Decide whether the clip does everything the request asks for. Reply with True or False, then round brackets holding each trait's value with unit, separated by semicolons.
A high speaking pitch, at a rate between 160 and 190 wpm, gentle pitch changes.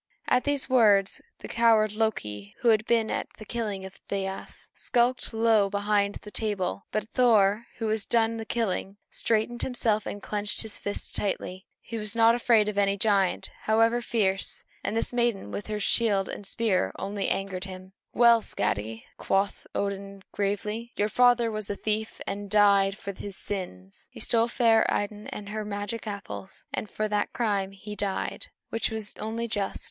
True (210 Hz; 175 wpm; 2.3 semitones)